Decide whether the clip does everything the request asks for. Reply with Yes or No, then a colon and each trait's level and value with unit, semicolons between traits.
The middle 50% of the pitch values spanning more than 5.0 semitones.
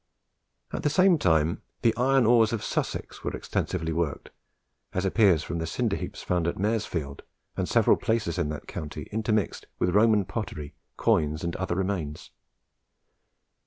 Yes: wide, 5.4 semitones